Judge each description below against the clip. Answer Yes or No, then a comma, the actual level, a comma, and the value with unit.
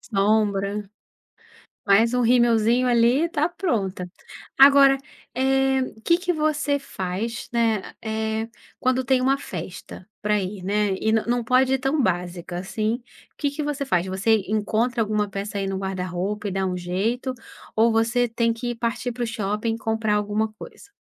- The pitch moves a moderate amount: Yes, average, 4.0 semitones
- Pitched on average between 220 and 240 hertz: Yes, high, 225 Hz